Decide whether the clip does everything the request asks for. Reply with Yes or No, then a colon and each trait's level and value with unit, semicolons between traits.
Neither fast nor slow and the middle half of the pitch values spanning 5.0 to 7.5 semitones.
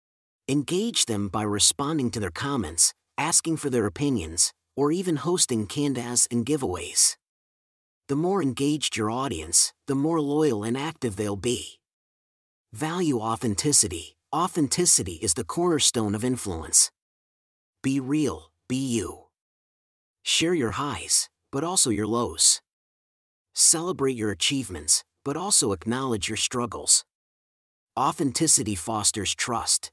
No: slow, 120 wpm; wide, 5.6 semitones